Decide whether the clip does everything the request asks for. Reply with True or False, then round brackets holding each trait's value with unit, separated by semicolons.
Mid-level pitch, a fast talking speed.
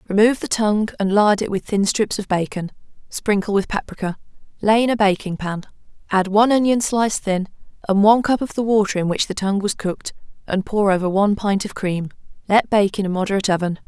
False (200 Hz; 210 wpm)